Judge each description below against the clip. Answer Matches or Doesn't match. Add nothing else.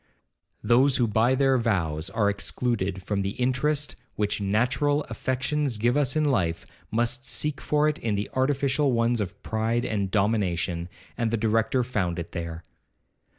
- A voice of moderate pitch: Doesn't match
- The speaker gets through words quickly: Doesn't match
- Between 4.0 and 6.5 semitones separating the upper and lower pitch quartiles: Matches